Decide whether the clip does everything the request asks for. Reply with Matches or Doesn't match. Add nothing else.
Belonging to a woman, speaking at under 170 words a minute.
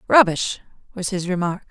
Matches